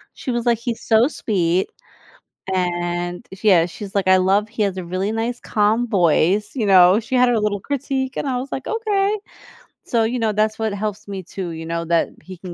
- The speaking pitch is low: No, high, 210 Hz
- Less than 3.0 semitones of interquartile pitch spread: No, average, 4.4 semitones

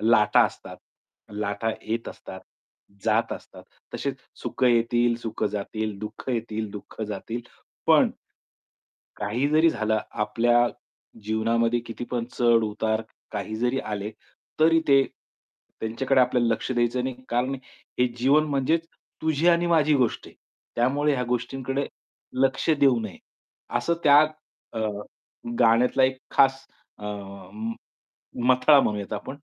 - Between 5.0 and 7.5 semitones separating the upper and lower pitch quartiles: No, average, 3.5 semitones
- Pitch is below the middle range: Yes, low, 120 Hz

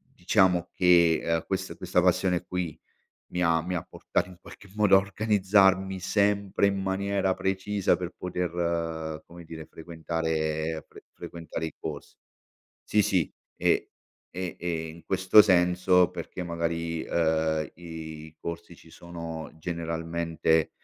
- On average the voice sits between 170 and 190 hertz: No, very low, 85 Hz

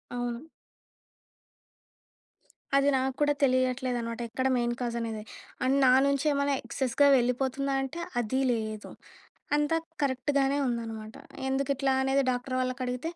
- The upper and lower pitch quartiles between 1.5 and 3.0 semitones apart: Yes, narrow, 2.4 semitones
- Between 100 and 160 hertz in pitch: No, very high, 255 Hz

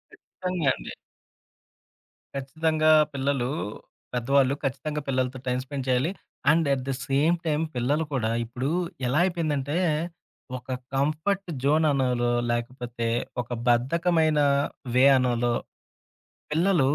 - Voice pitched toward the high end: No, low, 135 Hz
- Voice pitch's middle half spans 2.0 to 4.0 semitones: Yes, average, 3.7 semitones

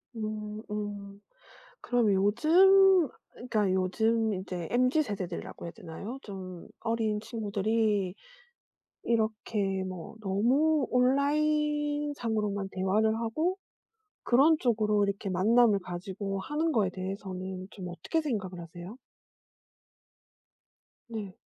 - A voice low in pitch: No, high, 215 Hz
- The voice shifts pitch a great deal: No, average, 4.4 semitones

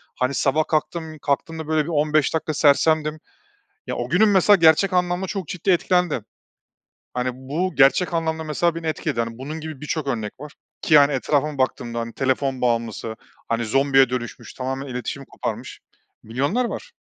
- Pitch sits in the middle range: Yes, medium, 150 Hz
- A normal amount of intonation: Yes, average, 3.8 semitones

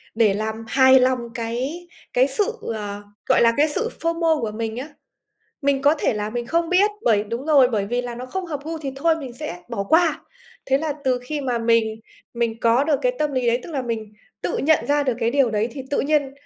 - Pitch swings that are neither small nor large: Yes, average, 4.7 semitones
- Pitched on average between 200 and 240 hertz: No, very high, 260 Hz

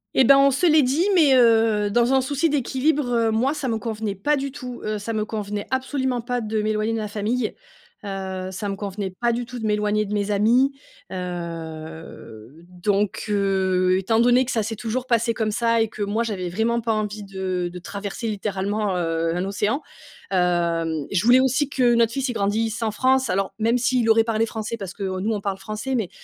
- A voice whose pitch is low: No, high, 215 Hz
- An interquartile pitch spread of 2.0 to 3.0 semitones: No, average, 3.6 semitones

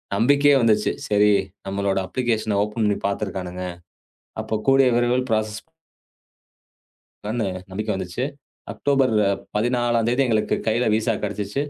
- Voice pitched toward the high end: No, low, 110 Hz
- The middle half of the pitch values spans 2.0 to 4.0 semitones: Yes, average, 2.9 semitones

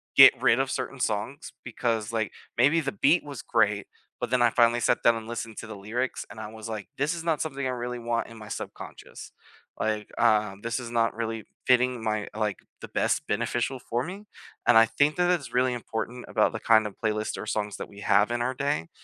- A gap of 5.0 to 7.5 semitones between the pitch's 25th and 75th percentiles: No, average, 2.9 semitones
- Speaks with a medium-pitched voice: No, low, 115 Hz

